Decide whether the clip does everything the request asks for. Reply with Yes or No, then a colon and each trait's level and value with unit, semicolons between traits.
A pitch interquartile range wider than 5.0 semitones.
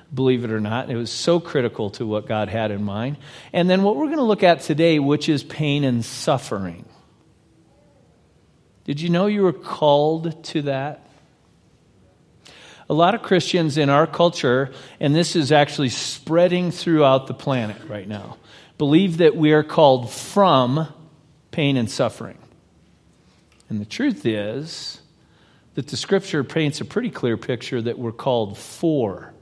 Yes: wide, 5.5 semitones